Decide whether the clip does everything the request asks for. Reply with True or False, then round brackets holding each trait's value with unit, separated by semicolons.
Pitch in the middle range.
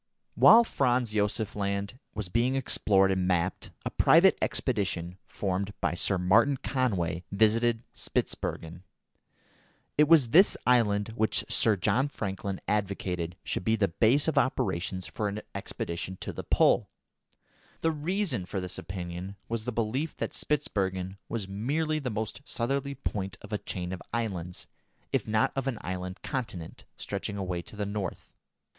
False (105 Hz)